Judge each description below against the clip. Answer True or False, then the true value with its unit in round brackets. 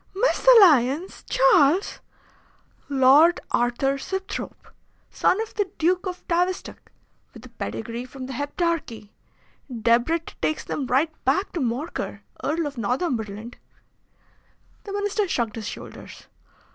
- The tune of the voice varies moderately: False (7.0 semitones)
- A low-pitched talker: False (300 Hz)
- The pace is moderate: False (115 wpm)